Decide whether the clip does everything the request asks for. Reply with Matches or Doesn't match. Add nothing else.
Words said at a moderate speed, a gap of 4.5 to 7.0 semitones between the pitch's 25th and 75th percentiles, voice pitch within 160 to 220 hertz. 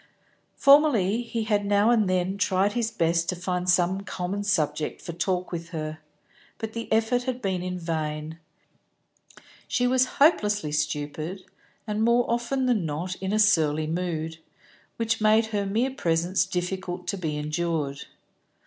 Matches